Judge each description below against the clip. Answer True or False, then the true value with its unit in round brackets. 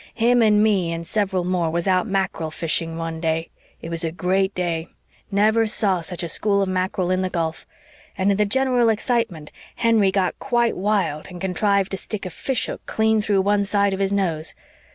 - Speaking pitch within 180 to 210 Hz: True (190 Hz)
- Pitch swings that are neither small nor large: True (3.5 semitones)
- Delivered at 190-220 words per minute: True (200 wpm)